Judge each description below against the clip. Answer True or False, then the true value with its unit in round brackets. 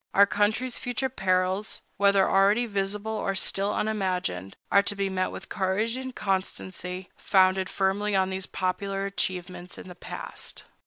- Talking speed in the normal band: True (150 wpm)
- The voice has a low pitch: False (195 Hz)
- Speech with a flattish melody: True (1.7 semitones)